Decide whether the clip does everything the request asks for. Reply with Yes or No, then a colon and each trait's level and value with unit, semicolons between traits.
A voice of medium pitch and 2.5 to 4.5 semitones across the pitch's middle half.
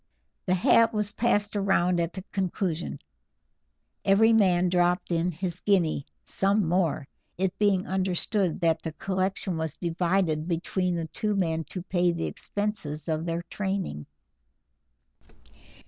Yes: medium, 180 Hz; average, 2.8 semitones